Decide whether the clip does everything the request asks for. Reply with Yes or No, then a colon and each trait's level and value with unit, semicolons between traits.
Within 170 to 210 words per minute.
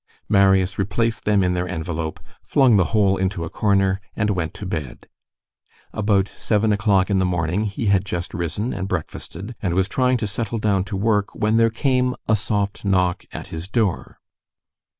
Yes: average, 180 wpm